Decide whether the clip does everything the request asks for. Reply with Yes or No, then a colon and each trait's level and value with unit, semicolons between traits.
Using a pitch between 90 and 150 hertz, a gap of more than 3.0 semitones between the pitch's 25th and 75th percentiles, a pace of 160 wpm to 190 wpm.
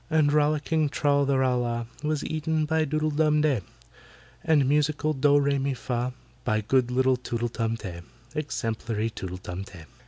Yes: medium, 140 Hz; average, 4.3 semitones; average, 165 wpm